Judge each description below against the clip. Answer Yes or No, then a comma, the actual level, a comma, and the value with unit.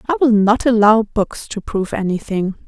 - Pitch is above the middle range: Yes, high, 210 Hz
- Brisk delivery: No, average, 180 wpm